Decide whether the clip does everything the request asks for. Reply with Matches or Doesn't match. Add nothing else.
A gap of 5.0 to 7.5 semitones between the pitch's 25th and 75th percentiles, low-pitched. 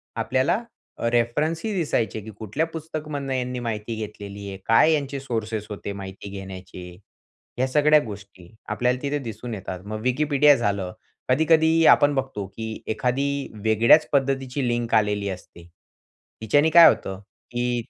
Matches